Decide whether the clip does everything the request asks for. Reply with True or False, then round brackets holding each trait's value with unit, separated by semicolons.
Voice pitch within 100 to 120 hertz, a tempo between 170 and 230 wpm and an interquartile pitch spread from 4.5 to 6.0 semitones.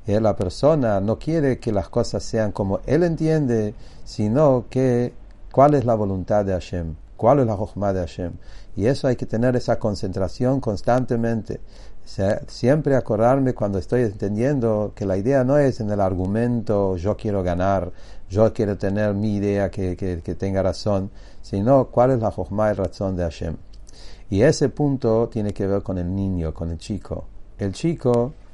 False (105 Hz; 175 wpm; 3.8 semitones)